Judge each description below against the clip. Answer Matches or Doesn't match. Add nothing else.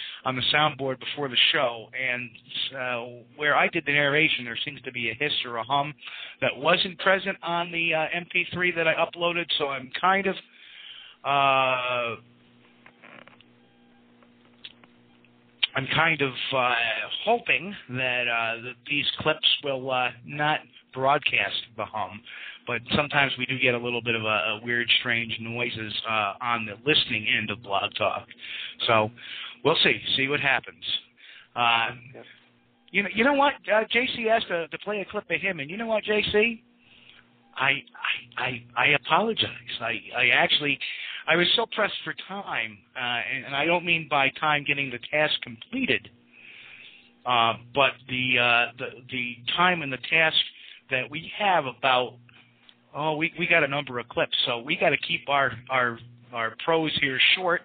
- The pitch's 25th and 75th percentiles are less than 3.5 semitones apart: Doesn't match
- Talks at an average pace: Matches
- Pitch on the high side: Doesn't match